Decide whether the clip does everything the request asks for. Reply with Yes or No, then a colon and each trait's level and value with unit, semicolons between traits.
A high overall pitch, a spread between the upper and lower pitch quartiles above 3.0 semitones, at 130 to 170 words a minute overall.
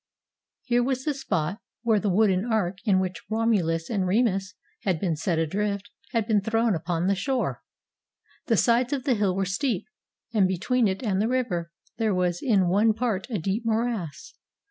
No: high, 205 Hz; average, 3.9 semitones; average, 180 wpm